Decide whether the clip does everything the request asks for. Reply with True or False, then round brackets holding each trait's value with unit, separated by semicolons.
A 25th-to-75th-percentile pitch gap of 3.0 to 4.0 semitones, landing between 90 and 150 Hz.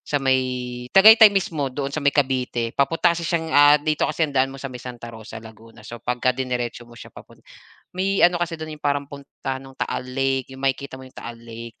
True (3.4 semitones; 135 Hz)